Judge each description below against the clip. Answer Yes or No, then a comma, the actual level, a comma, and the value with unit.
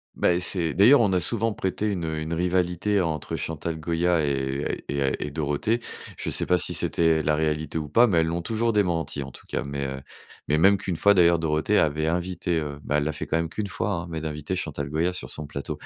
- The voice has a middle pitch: No, very low, 80 Hz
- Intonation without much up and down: No, average, 3.2 semitones